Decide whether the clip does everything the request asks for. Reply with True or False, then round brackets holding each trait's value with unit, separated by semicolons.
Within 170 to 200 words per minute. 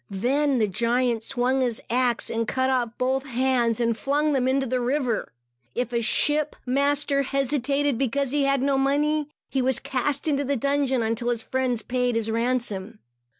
True (175 wpm)